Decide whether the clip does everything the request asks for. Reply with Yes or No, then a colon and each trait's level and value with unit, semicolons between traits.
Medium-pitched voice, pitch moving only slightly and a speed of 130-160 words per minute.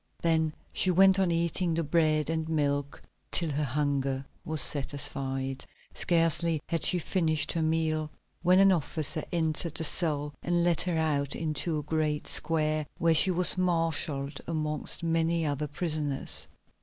Yes: medium, 160 Hz; narrow, 2.2 semitones; average, 150 wpm